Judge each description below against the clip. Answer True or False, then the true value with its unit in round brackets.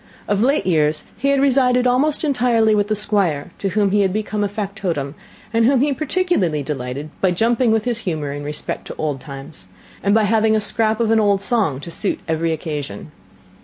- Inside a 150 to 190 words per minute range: False (200 wpm)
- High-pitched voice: True (205 Hz)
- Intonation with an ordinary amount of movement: False (6.6 semitones)